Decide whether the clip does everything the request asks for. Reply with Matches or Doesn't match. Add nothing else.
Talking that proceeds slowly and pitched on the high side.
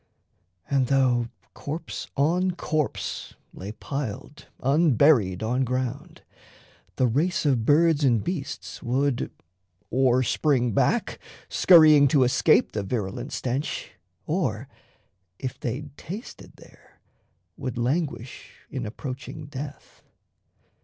Doesn't match